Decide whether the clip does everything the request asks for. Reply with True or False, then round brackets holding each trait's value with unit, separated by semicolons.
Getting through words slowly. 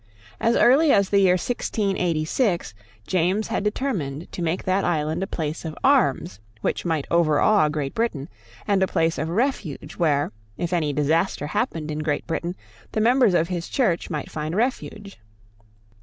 False (160 wpm)